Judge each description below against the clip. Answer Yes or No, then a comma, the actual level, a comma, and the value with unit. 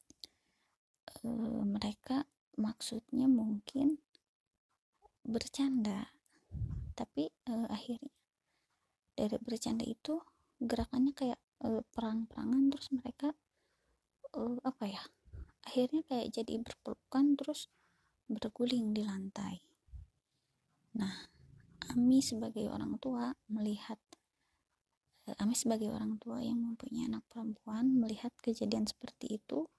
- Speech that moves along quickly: No, average, 95 wpm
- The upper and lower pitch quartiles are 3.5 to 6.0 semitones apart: No, average, 3.1 semitones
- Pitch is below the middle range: No, high, 235 Hz